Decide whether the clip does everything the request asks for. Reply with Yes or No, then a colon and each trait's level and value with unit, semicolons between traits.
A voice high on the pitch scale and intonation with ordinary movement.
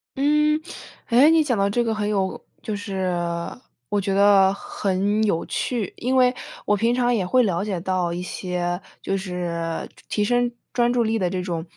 Yes: high, 205 Hz; average, 4.6 semitones